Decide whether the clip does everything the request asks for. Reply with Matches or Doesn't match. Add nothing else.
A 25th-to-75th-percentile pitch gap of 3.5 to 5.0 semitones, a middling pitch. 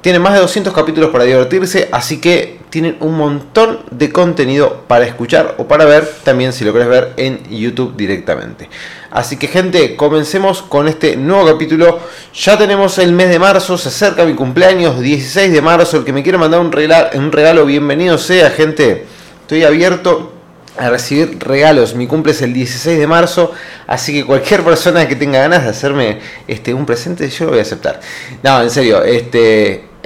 Matches